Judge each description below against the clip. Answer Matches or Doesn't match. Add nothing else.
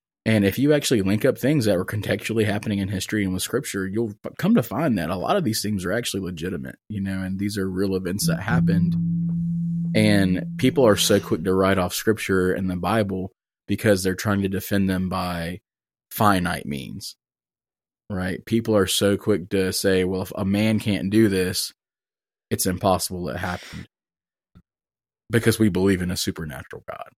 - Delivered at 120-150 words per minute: Doesn't match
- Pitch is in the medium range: Doesn't match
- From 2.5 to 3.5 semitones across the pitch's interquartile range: Matches